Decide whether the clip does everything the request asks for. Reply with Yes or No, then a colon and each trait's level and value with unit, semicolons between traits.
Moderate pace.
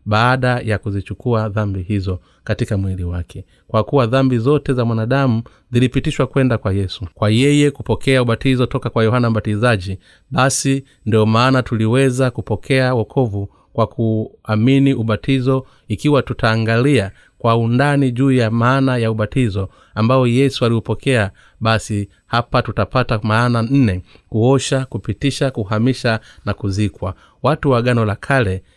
Yes: average, 130 wpm